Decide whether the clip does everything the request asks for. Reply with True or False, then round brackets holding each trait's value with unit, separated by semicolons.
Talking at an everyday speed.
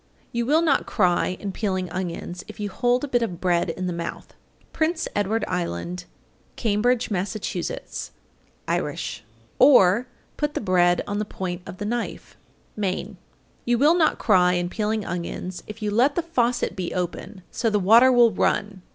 True (175 wpm)